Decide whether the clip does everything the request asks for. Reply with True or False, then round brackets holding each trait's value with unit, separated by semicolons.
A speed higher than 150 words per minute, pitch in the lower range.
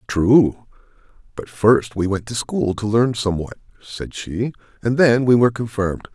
True (165 wpm; 110 Hz)